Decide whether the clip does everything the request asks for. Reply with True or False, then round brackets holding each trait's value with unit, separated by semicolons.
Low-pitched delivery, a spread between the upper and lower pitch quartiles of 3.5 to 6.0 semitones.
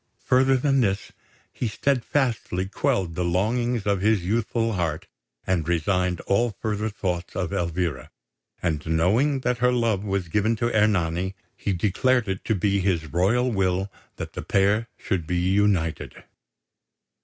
True (100 Hz; 4.3 semitones)